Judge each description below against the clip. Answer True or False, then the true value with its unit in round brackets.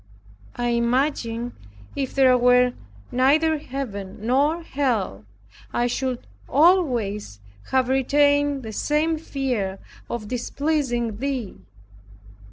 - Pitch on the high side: True (255 Hz)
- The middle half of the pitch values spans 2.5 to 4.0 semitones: True (3.3 semitones)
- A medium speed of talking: False (95 wpm)